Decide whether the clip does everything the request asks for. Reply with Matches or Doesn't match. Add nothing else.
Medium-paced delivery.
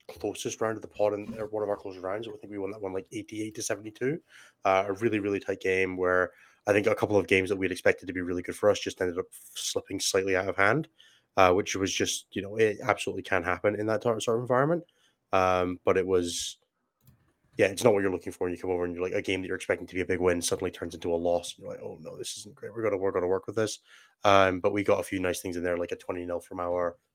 Doesn't match